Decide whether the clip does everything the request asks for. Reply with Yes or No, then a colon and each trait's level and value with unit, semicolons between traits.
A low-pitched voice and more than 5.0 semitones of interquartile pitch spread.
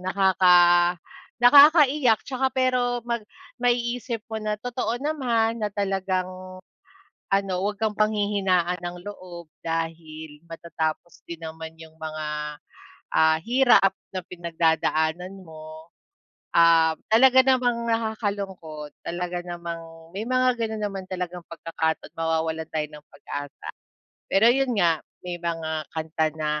No: medium, 180 Hz; wide, 5.4 semitones